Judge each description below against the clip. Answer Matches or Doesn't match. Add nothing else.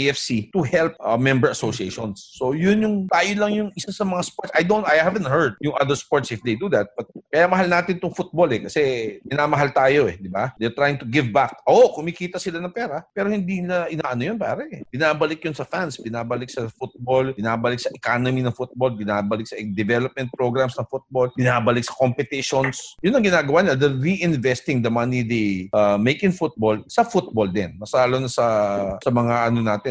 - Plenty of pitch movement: Matches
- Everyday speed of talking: Doesn't match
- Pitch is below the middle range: Matches